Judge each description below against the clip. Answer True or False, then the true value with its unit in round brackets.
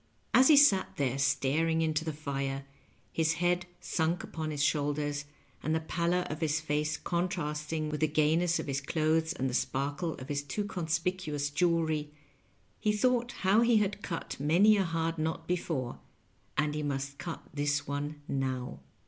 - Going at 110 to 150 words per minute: False (170 wpm)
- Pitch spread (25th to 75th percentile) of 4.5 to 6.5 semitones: False (3.1 semitones)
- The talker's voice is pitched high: False (155 Hz)